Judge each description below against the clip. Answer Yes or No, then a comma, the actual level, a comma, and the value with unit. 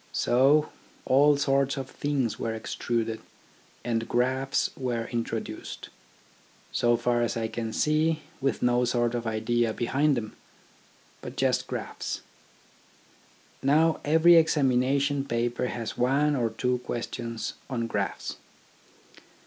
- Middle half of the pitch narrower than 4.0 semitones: Yes, average, 3.0 semitones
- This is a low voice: Yes, low, 125 Hz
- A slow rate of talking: Yes, slow, 115 wpm